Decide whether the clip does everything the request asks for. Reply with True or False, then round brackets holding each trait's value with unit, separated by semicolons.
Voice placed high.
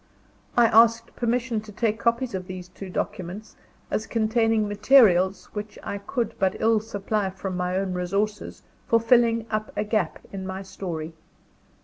True (210 Hz)